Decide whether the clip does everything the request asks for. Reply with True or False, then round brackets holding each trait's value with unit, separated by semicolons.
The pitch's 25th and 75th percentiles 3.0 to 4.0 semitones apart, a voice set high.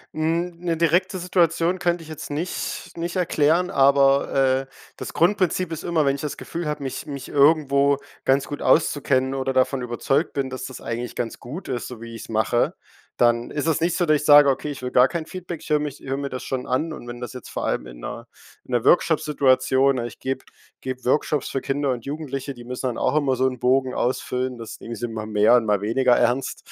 False (3.7 semitones; 135 Hz)